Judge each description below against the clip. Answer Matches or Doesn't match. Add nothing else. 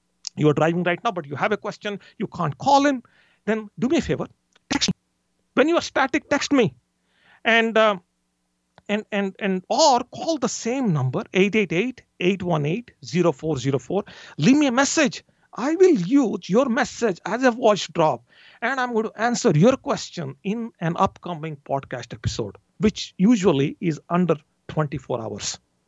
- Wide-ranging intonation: Matches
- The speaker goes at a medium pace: Matches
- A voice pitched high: Matches